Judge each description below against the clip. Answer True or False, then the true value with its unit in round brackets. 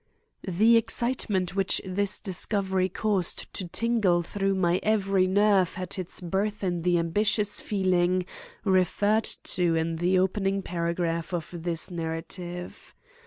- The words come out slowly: True (130 wpm)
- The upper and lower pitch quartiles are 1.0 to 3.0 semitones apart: True (2.6 semitones)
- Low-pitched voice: False (185 Hz)